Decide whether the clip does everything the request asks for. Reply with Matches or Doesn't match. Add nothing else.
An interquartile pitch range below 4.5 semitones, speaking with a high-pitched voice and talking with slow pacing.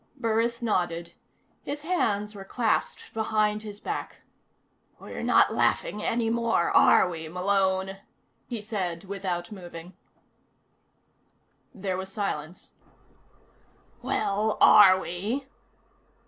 Matches